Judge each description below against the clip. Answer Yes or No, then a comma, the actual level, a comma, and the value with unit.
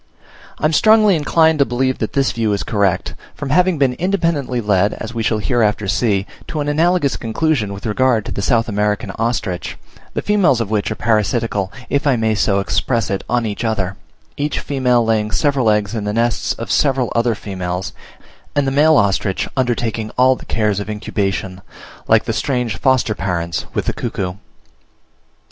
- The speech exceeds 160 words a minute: Yes, average, 180 wpm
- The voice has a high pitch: No, low, 115 Hz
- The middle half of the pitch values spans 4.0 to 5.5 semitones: Yes, average, 4.6 semitones